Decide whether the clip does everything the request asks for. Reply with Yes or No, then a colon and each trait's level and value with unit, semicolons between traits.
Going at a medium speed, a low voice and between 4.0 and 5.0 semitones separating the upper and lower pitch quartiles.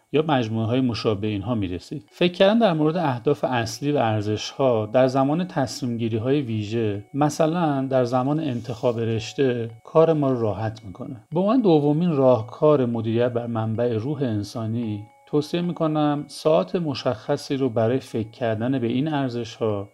Yes: average, 145 wpm; low, 130 Hz; average, 4.6 semitones